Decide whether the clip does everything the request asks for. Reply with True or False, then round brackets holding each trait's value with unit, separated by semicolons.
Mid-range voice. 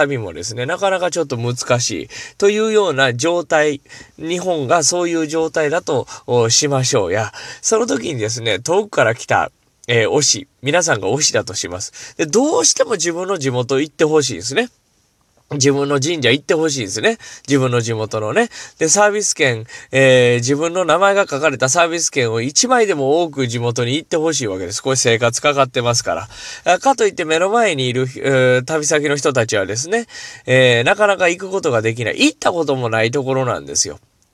True (145 Hz)